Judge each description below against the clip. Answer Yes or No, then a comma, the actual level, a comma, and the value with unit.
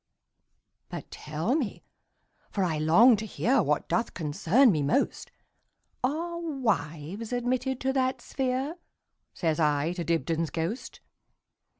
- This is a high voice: Yes, high, 220 Hz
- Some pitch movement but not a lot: No, wide, 8.4 semitones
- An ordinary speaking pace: No, slow, 105 wpm